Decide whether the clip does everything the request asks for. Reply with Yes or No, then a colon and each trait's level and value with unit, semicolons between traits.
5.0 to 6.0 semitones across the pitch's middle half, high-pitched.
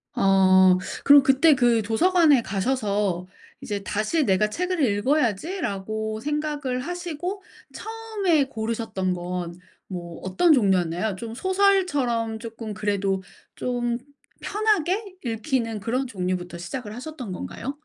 No: wide, 7.2 semitones; high, 230 Hz